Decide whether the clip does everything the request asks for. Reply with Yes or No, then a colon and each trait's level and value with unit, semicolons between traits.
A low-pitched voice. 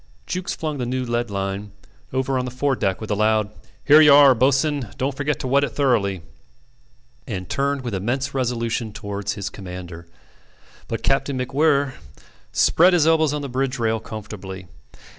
Yes: low, 125 Hz